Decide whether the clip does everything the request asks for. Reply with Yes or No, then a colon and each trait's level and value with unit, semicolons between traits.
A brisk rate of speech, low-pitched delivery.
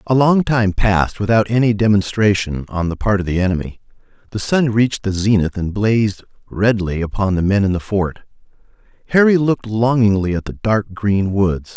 No: average, 180 wpm; low, 105 Hz